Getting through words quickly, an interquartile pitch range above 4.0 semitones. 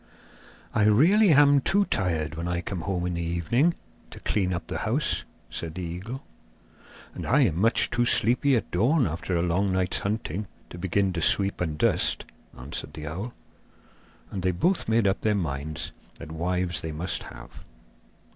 No: average, 175 wpm; average, 5.1 semitones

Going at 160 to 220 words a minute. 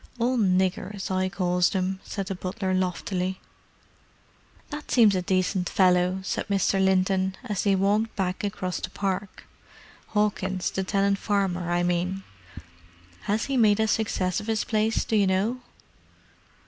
No: average, 150 wpm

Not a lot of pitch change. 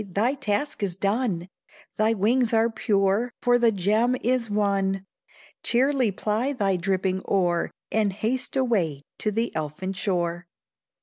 No: average, 3.8 semitones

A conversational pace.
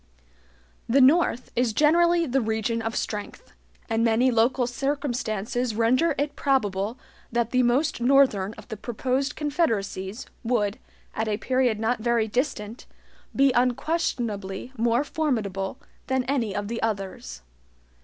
No: slow, 130 wpm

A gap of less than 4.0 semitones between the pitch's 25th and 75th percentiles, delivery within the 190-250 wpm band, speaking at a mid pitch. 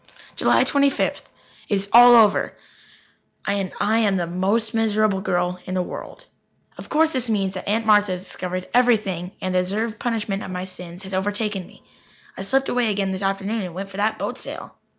No: average, 3.2 semitones; average, 195 wpm; high, 200 Hz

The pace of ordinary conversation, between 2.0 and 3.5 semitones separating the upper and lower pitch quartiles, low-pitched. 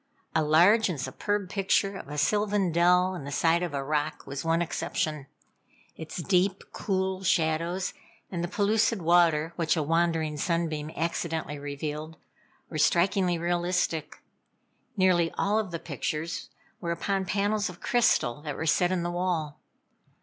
No: average, 150 wpm; average, 3.0 semitones; medium, 170 Hz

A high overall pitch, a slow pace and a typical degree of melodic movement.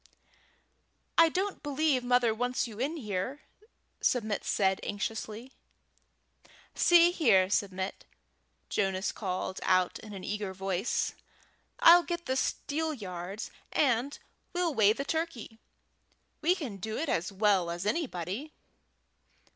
No: high, 225 Hz; slow, 115 wpm; wide, 7.4 semitones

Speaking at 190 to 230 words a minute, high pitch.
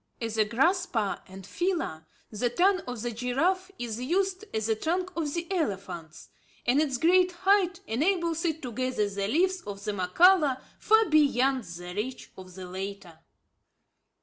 No: average, 160 wpm; very high, 255 Hz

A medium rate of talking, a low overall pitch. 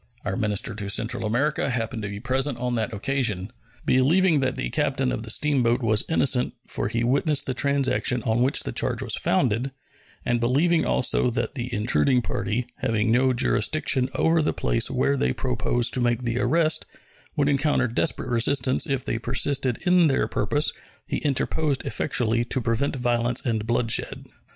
Yes: average, 170 wpm; low, 125 Hz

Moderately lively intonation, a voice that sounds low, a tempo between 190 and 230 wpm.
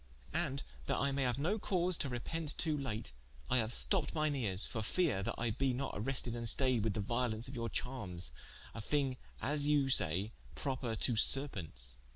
Yes: average, 4.5 semitones; low, 125 Hz; average, 195 wpm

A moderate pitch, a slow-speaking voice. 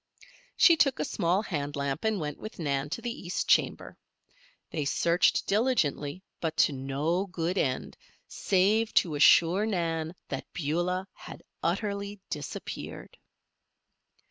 Yes: medium, 170 Hz; slow, 130 wpm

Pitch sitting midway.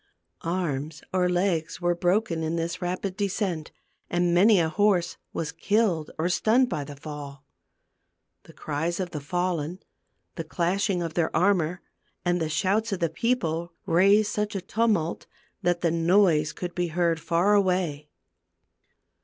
Yes: medium, 175 Hz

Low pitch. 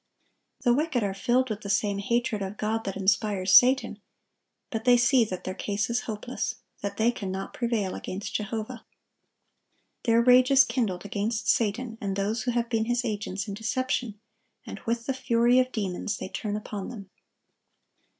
No: high, 220 Hz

